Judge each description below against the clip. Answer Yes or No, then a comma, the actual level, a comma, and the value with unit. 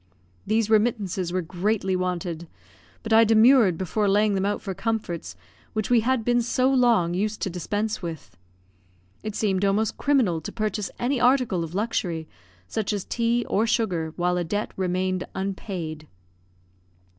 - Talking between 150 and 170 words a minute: Yes, average, 155 wpm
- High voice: Yes, high, 205 Hz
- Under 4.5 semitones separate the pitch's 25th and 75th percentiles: Yes, average, 3.8 semitones